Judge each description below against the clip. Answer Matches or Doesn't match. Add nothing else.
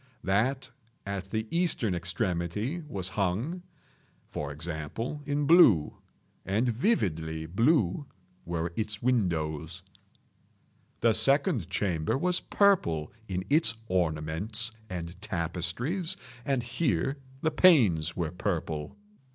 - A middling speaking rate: Doesn't match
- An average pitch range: Doesn't match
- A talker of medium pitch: Doesn't match